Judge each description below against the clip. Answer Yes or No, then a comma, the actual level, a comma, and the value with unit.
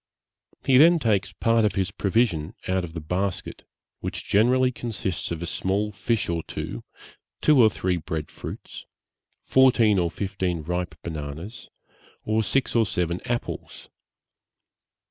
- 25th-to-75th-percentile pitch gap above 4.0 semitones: Yes, average, 5.1 semitones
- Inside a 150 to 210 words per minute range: No, average, 140 wpm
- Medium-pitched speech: No, very low, 95 Hz